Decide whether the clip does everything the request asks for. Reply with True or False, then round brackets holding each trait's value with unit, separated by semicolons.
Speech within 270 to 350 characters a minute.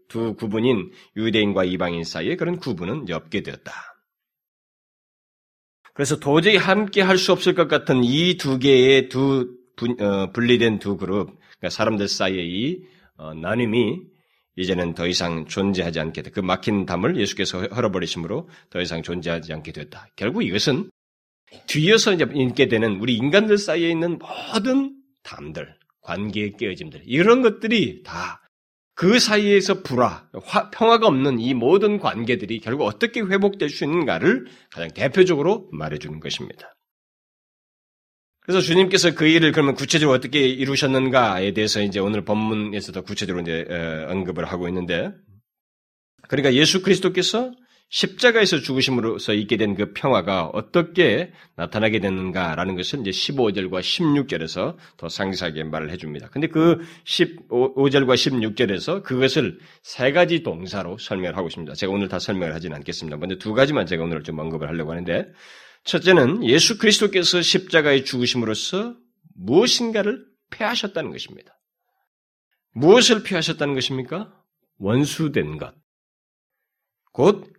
True (325 characters per minute)